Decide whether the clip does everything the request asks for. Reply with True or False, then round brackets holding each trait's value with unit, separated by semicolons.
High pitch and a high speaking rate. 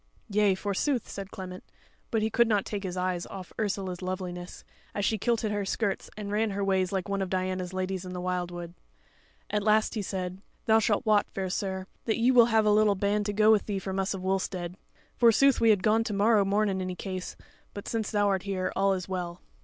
True (195 Hz; 225 wpm)